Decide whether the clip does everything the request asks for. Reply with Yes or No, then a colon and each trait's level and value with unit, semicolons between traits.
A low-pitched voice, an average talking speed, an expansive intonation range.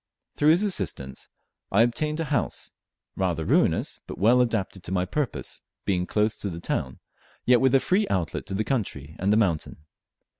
Yes: low, 105 Hz; average, 180 wpm; wide, 6.7 semitones